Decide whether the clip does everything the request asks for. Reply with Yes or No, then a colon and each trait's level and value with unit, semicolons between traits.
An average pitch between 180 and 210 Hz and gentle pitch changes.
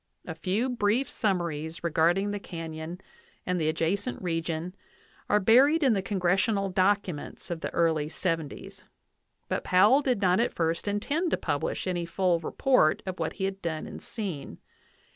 No: medium, 185 Hz; average, 3.8 semitones